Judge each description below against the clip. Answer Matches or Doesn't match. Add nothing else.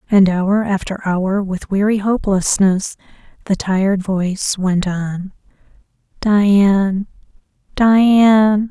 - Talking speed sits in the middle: Doesn't match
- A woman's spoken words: Matches